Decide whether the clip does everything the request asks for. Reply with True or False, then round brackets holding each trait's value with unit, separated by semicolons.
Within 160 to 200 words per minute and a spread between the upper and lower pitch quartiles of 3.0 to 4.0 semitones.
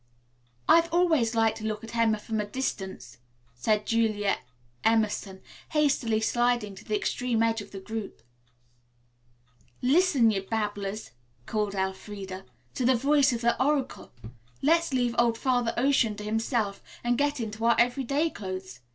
False (150 wpm; 3.4 semitones)